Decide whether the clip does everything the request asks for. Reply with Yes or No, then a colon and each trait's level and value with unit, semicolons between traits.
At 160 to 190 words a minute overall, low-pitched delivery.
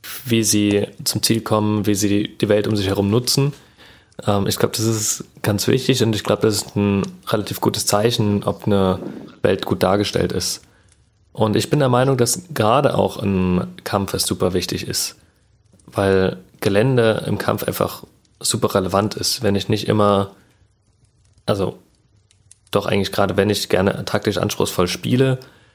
Yes: average, 165 wpm; low, 105 Hz